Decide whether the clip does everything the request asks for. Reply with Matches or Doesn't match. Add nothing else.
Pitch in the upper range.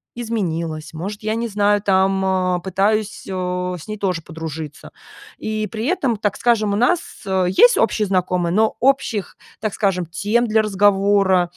Matches